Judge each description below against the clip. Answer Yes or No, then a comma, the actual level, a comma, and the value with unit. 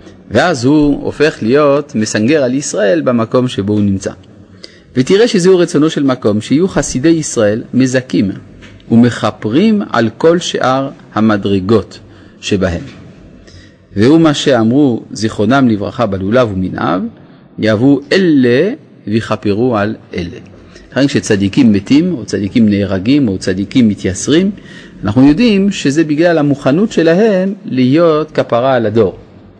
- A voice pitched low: Yes, low, 125 Hz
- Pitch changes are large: Yes, wide, 6.7 semitones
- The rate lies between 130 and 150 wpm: No, average, 115 wpm